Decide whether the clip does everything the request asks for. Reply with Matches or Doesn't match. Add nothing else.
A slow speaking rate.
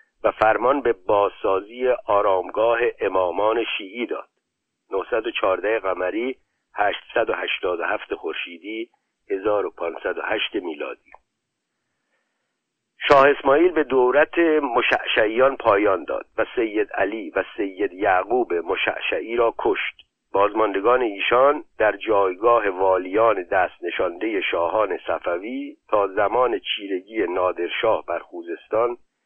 Matches